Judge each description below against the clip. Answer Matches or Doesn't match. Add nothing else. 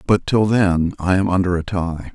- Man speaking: Matches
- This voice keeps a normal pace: Doesn't match